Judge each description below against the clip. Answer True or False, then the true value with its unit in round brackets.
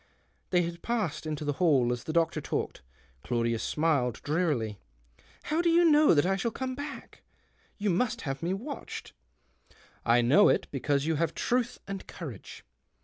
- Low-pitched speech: False (165 Hz)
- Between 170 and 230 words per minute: True (175 wpm)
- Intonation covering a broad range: True (7.7 semitones)